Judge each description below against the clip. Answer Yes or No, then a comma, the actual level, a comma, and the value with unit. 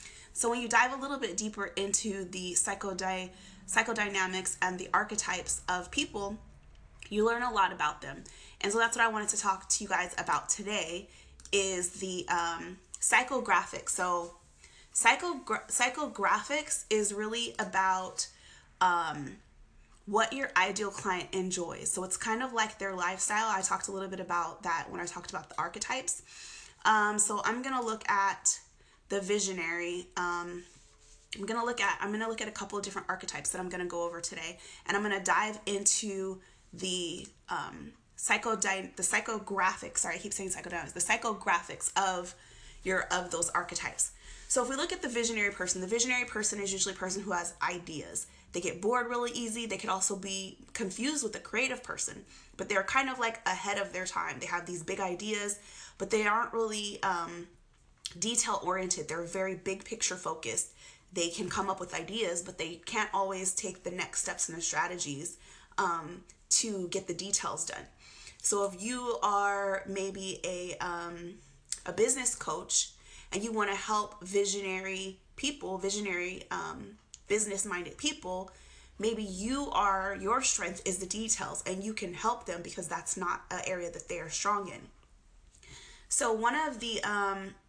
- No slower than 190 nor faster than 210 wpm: No, average, 175 wpm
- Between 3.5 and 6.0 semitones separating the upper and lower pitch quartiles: No, average, 3.0 semitones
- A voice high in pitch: Yes, high, 195 Hz